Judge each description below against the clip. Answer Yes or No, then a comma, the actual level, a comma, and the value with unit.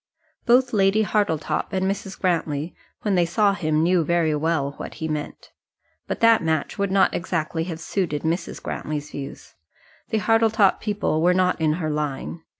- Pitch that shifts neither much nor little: Yes, average, 4.1 semitones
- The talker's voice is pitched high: No, medium, 175 Hz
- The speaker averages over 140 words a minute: Yes, average, 165 wpm